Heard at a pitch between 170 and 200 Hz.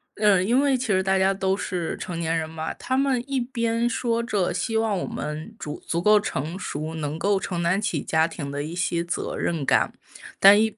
Yes: high, 190 Hz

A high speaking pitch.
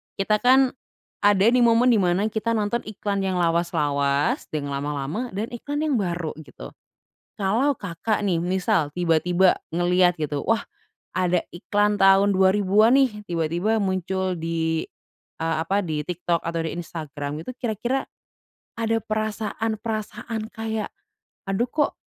Yes: high, 195 Hz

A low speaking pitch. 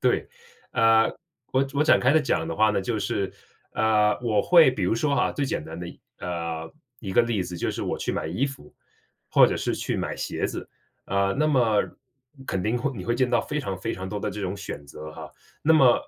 Yes: low, 110 Hz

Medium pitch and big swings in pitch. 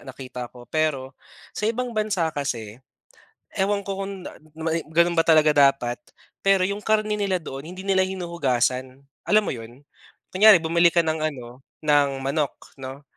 Yes: medium, 160 Hz; wide, 6.2 semitones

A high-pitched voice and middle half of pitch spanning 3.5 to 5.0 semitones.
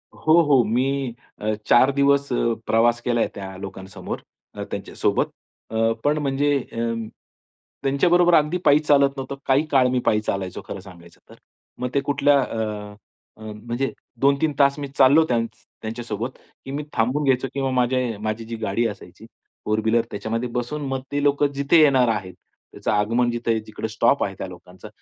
No: low, 125 Hz; average, 4.2 semitones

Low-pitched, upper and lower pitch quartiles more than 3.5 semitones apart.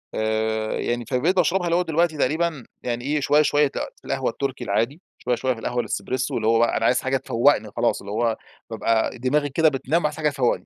Yes: low, 130 Hz; average, 4.5 semitones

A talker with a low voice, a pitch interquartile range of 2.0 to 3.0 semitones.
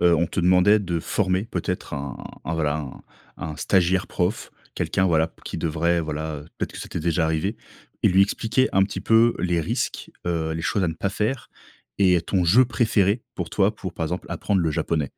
No: very low, 90 Hz; average, 3.5 semitones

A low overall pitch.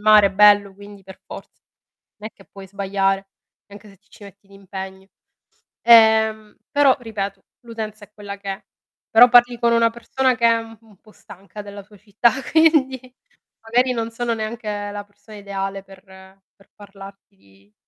No: high, 205 Hz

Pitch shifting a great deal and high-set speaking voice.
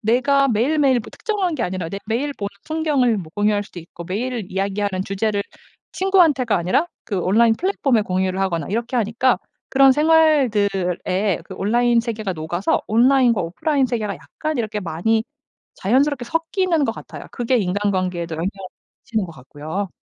Yes: wide, 5.8 semitones; high, 220 Hz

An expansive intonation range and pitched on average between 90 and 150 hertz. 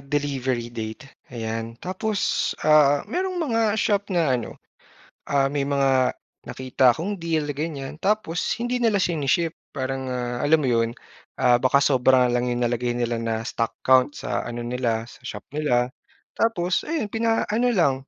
Yes: wide, 6.3 semitones; medium, 140 Hz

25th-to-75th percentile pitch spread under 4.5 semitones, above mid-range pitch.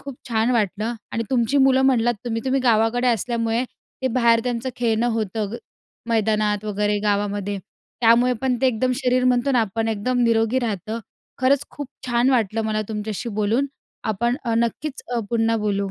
Yes: narrow, 2.6 semitones; high, 230 Hz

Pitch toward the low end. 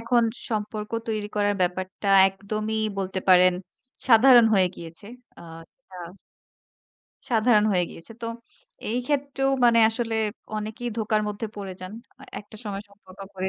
No: high, 210 Hz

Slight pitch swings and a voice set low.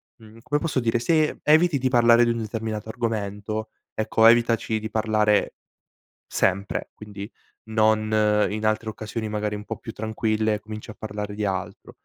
Yes: narrow, 1.5 semitones; low, 110 Hz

